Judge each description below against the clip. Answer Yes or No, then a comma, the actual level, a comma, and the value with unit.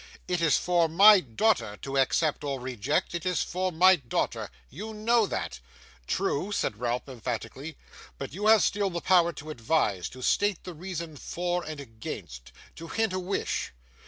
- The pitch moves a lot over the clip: Yes, wide, 6.3 semitones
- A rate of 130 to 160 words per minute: No, average, 170 wpm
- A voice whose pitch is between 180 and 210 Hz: No, medium, 165 Hz